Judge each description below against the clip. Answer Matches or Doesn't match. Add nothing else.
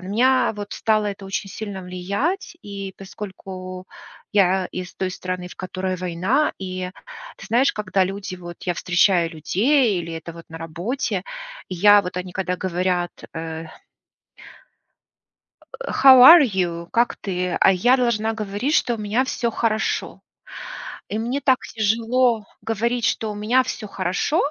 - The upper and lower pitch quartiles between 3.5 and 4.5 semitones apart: Matches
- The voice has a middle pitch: Doesn't match